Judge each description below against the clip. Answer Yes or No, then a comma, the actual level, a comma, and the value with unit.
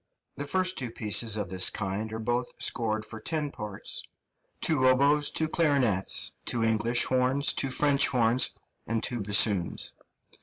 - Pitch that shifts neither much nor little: Yes, average, 4.5 semitones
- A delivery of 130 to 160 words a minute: Yes, average, 150 wpm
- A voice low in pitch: Yes, low, 120 Hz